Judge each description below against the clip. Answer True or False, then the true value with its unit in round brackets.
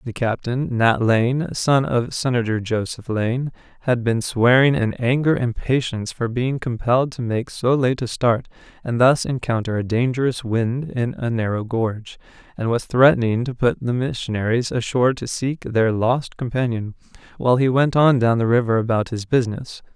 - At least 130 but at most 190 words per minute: True (170 wpm)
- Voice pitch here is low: True (120 Hz)